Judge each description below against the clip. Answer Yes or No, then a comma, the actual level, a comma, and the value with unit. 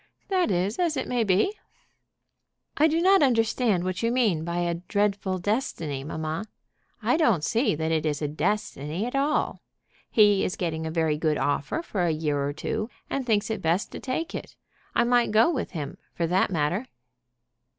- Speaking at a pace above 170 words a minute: Yes, average, 185 wpm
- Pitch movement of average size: No, wide, 7.1 semitones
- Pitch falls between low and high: No, high, 195 Hz